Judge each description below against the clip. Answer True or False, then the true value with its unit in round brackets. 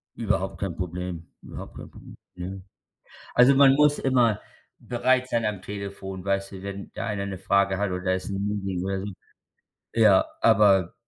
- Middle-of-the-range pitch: False (100 Hz)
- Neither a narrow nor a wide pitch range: False (2.2 semitones)